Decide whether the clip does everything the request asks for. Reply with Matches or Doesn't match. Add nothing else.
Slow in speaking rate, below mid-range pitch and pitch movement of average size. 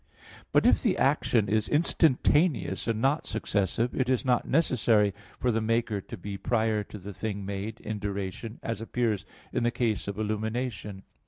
Doesn't match